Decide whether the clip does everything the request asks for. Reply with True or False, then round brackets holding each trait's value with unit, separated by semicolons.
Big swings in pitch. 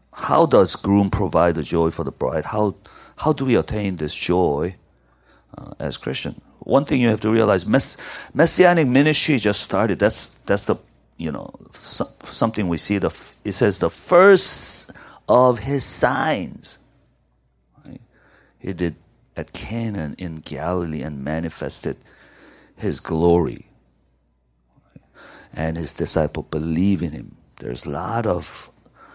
True (6.7 semitones)